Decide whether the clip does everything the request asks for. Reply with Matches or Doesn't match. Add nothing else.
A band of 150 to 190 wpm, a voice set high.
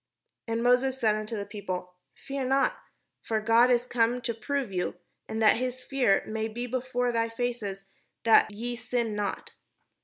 Matches